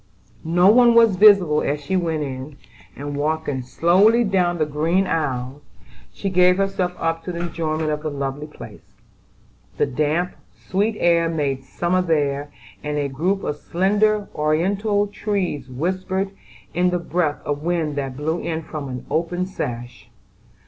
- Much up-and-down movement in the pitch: No, average, 4.1 semitones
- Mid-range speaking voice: Yes, medium, 165 Hz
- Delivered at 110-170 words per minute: Yes, average, 155 wpm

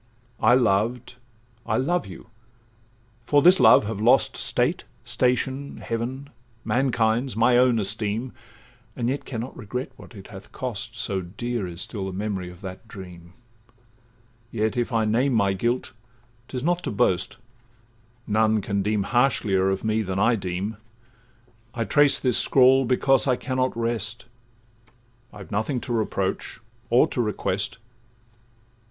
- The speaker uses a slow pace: No, average, 145 wpm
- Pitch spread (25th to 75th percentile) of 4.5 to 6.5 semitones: No, average, 4.0 semitones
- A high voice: No, low, 115 Hz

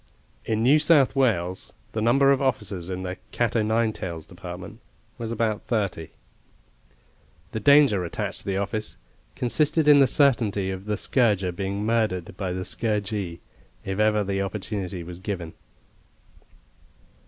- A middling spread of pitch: Yes, average, 3.9 semitones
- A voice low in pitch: Yes, low, 105 Hz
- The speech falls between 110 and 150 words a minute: Yes, average, 145 wpm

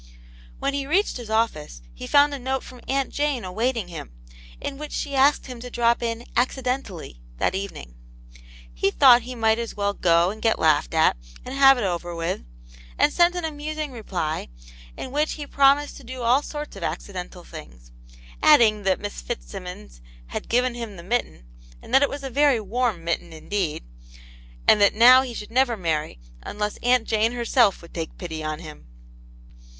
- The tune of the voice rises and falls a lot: Yes, wide, 6.9 semitones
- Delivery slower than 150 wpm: No, average, 185 wpm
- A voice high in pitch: Yes, high, 230 Hz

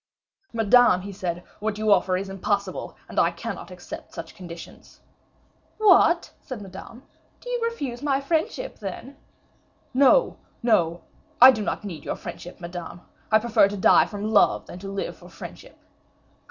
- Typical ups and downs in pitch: No, wide, 5.8 semitones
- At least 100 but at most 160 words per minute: Yes, average, 155 wpm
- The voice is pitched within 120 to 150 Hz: No, high, 210 Hz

